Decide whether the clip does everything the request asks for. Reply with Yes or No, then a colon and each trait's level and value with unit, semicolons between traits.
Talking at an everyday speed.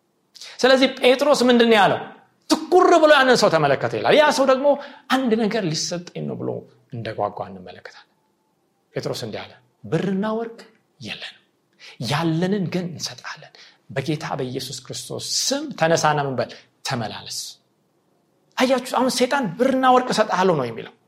No: fast, 125 wpm